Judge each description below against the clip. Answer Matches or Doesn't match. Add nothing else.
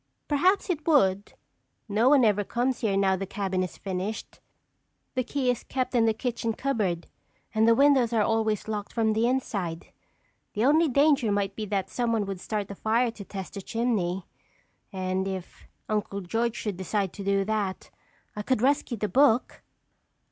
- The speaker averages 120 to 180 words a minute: Matches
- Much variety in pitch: Doesn't match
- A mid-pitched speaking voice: Doesn't match